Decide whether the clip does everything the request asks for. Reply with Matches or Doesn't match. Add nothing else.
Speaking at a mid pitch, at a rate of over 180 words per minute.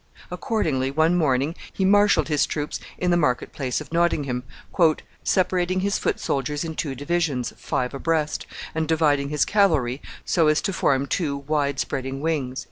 Doesn't match